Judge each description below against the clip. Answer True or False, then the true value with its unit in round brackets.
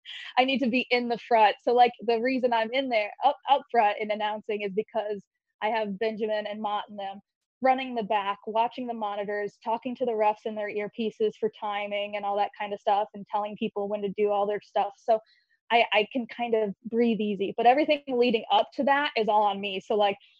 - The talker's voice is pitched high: True (220 Hz)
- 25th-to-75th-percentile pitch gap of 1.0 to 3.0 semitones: True (2.6 semitones)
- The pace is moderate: False (230 wpm)